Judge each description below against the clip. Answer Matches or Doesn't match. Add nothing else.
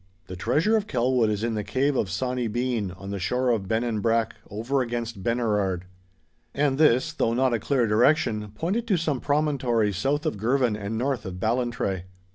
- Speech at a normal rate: Matches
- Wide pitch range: Doesn't match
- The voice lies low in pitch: Matches